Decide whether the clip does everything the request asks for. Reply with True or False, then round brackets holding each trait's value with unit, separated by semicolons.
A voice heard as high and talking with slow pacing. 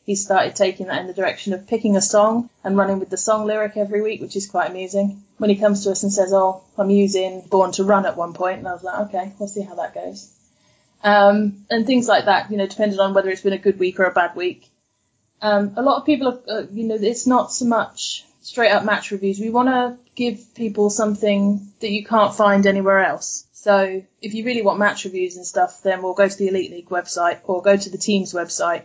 False (200 Hz; 250 wpm)